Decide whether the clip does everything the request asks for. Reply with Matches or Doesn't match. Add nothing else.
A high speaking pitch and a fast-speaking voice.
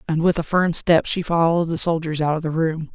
Doesn't match